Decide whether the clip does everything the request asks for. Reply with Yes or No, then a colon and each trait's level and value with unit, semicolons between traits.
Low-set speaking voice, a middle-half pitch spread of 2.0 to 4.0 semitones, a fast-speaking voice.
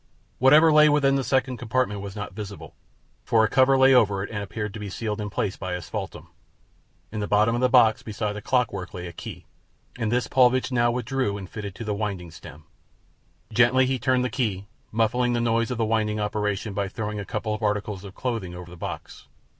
Yes: low, 110 Hz; average, 3.5 semitones; fast, 215 wpm